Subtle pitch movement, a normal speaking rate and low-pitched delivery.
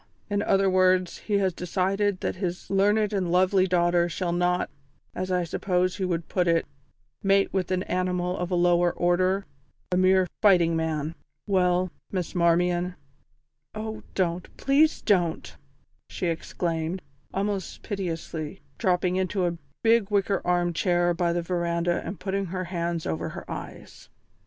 No: narrow, 1.8 semitones; average, 150 wpm; medium, 180 Hz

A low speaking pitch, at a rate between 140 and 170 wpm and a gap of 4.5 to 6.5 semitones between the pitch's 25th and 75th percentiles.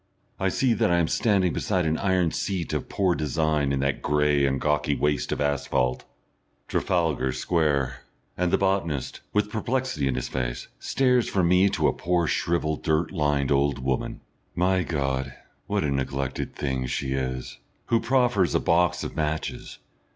Yes: very low, 80 Hz; average, 165 wpm; average, 5.0 semitones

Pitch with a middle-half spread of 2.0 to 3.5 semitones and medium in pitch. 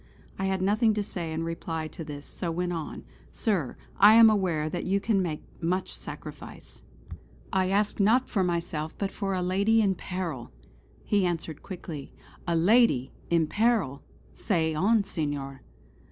No: average, 4.0 semitones; medium, 180 Hz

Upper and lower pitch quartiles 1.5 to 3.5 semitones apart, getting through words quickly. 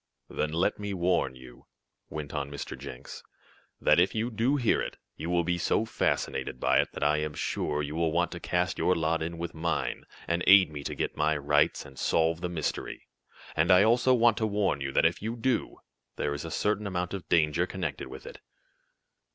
No: average, 4.4 semitones; fast, 210 wpm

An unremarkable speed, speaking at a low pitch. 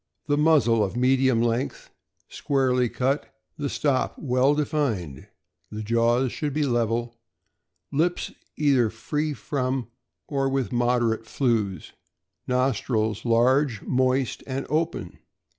No: slow, 110 wpm; low, 125 Hz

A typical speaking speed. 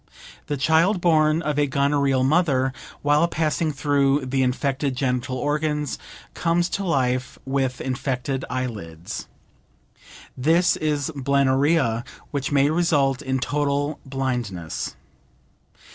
No: slow, 110 wpm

